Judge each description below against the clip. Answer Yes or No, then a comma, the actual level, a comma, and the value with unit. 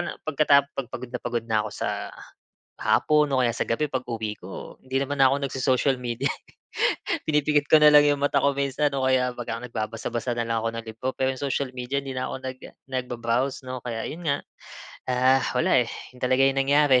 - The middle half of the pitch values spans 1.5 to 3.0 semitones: Yes, average, 2.7 semitones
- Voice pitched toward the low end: Yes, low, 130 Hz